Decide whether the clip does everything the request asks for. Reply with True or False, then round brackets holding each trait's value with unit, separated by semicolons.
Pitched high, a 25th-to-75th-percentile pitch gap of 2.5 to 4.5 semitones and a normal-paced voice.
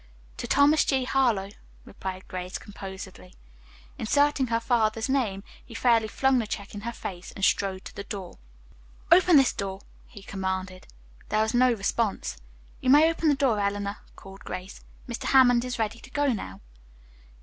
False (220 Hz; 4.9 semitones; 165 wpm)